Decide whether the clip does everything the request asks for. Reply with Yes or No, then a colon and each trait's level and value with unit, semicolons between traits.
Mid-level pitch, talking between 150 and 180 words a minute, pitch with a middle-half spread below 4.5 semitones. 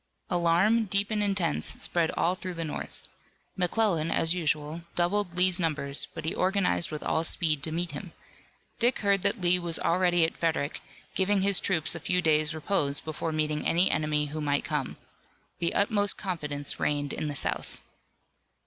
Yes: medium, 170 Hz; average, 170 wpm; average, 3.5 semitones